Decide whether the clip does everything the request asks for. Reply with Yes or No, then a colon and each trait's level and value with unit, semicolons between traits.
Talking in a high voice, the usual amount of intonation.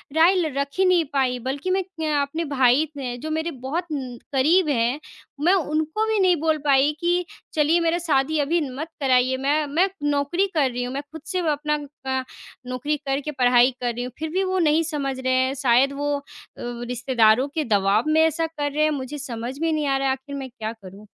Yes: very high, 285 Hz; average, 3.6 semitones